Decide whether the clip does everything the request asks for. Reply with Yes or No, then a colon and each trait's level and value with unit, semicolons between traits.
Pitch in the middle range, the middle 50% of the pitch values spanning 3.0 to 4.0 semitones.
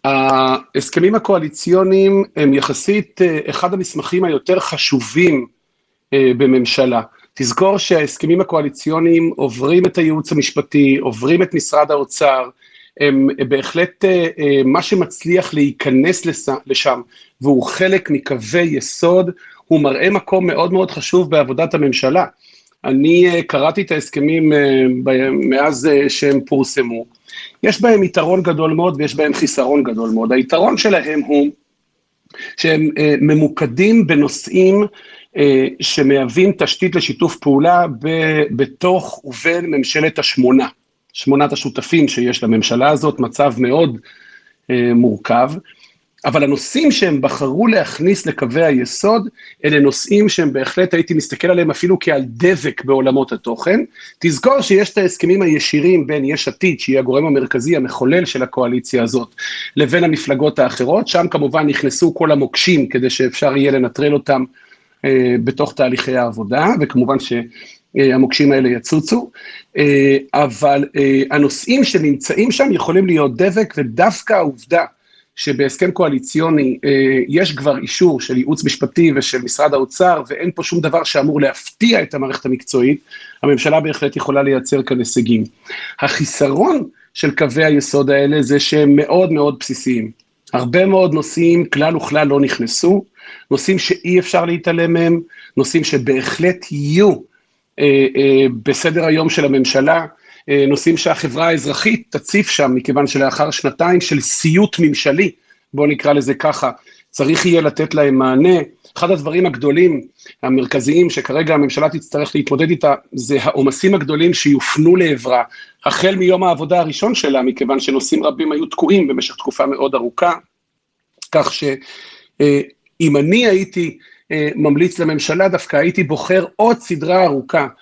No: medium, 150 Hz; average, 4.4 semitones